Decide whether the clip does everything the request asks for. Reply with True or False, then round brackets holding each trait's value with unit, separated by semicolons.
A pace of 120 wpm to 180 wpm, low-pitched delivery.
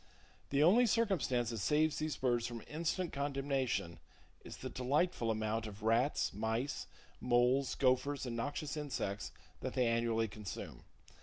True (140 wpm; 125 Hz)